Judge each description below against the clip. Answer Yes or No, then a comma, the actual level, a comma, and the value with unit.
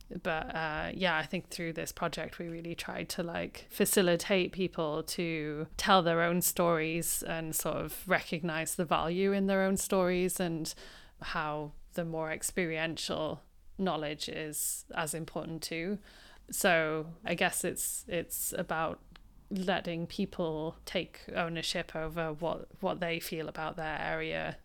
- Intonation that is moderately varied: No, narrow, 2.3 semitones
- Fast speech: No, average, 140 wpm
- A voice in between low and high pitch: Yes, medium, 165 Hz